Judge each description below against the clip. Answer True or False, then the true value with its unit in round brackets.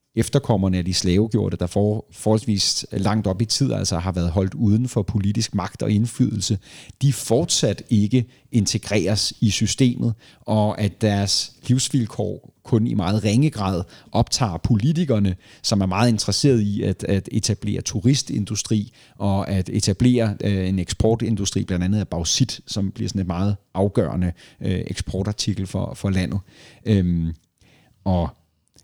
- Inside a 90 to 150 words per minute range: True (145 wpm)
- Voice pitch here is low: True (105 Hz)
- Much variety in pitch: False (3.1 semitones)